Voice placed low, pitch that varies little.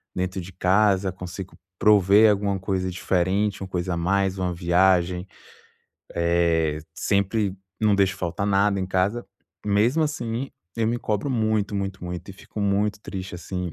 Yes: very low, 95 Hz; narrow, 2.3 semitones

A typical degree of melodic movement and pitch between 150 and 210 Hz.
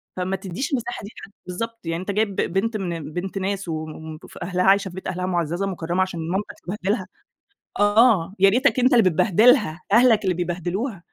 Yes: average, 3.4 semitones; high, 190 Hz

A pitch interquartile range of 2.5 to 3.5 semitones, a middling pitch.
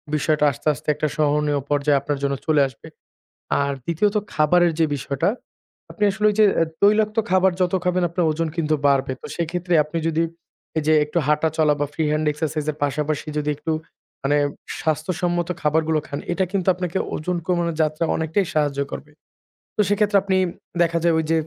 Yes: average, 3.0 semitones; medium, 160 Hz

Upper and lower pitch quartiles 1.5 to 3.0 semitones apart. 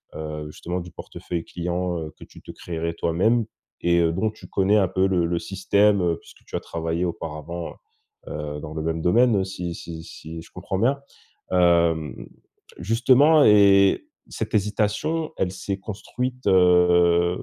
No: average, 3.5 semitones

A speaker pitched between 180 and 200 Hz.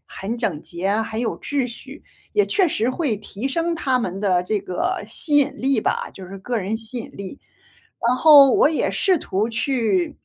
No: high, 235 Hz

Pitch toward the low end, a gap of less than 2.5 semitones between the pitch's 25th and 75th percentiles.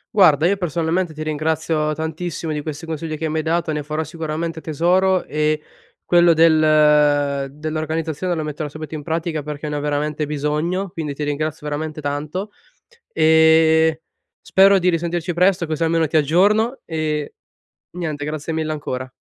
No: medium, 155 Hz; narrow, 1.7 semitones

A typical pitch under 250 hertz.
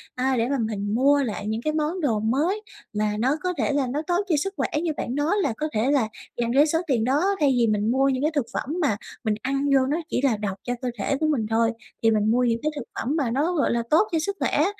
No: very high, 265 Hz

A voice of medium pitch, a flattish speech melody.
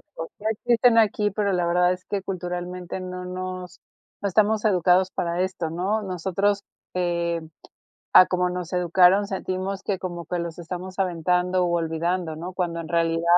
Yes: medium, 180 Hz; narrow, 1.7 semitones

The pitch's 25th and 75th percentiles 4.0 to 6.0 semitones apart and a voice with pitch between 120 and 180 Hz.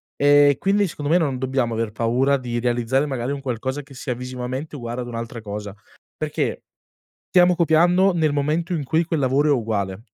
Yes: average, 4.3 semitones; low, 135 Hz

